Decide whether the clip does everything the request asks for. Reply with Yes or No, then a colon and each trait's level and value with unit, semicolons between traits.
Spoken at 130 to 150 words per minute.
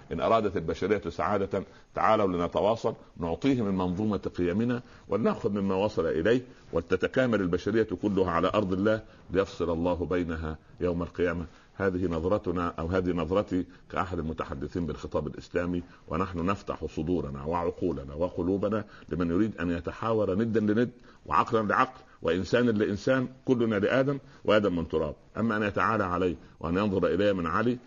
Yes: fast, 135 wpm